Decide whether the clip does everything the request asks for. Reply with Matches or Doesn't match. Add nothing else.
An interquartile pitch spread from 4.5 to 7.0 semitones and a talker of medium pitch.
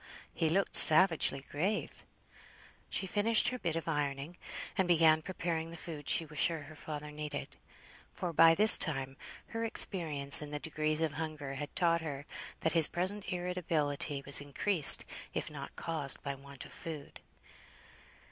Doesn't match